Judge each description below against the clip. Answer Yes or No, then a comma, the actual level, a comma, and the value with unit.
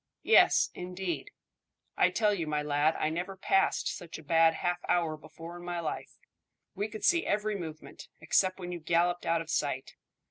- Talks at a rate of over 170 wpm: Yes, average, 180 wpm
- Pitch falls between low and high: Yes, medium, 175 Hz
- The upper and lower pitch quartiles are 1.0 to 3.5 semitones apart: Yes, average, 2.9 semitones